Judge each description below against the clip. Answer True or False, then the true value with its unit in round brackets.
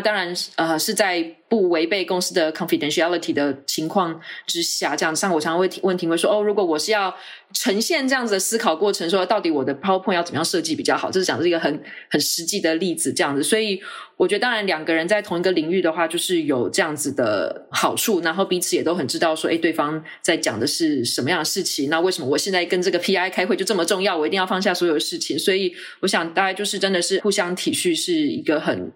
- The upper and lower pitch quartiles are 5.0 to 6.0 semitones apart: False (3.8 semitones)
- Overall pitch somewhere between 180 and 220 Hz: True (185 Hz)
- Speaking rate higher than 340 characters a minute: True (410 characters per minute)